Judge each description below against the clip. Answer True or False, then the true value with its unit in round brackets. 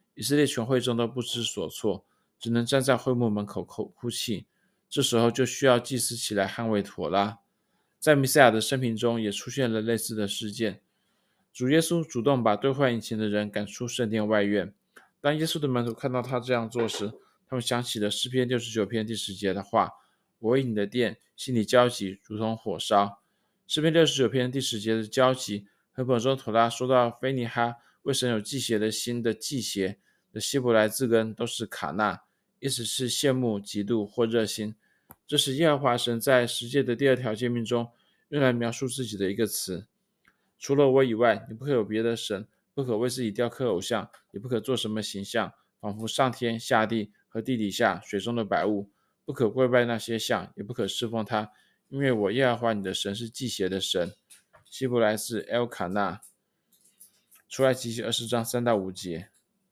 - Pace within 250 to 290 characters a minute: True (280 characters per minute)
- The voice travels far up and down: False (3.1 semitones)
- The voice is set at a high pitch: False (115 Hz)